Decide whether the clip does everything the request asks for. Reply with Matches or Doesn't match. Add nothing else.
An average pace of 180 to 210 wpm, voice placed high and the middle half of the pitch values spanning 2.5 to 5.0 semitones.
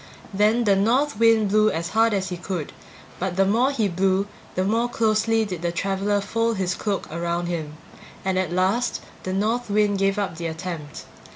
Matches